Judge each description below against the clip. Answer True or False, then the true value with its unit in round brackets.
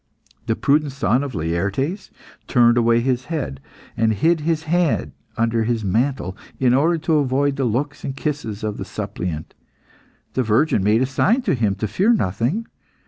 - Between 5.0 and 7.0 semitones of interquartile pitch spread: True (5.4 semitones)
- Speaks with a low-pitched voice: True (125 Hz)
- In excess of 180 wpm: False (170 wpm)